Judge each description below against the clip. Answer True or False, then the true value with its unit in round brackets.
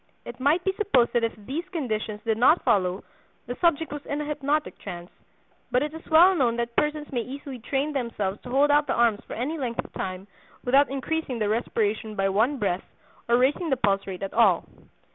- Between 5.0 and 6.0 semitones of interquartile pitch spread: True (5.4 semitones)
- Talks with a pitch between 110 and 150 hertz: False (250 Hz)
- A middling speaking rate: False (210 wpm)